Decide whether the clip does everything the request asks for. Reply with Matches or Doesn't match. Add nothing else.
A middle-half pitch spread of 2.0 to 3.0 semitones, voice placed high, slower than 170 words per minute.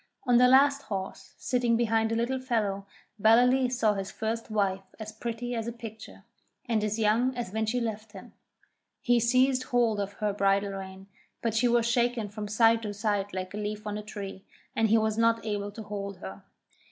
Doesn't match